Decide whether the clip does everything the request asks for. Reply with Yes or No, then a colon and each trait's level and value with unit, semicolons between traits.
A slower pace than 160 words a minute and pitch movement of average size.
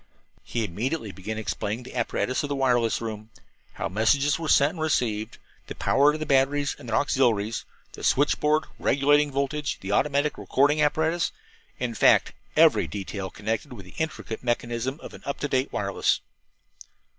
No: average, 170 wpm; average, 4.8 semitones